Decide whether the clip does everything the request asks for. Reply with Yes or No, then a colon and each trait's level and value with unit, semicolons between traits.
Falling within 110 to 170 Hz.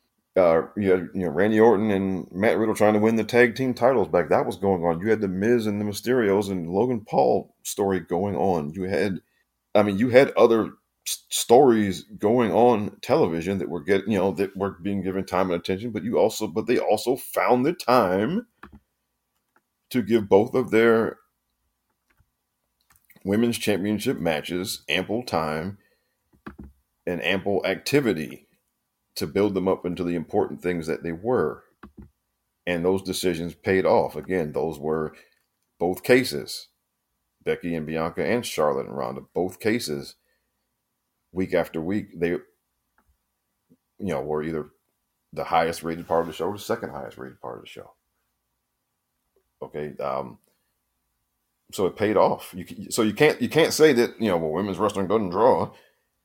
No: very low, 95 Hz